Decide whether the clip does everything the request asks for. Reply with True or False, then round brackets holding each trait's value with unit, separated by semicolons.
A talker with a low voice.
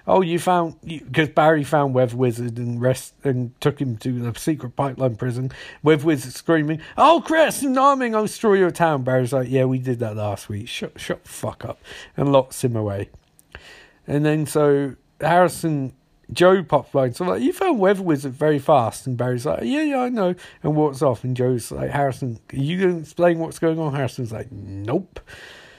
False (145 Hz)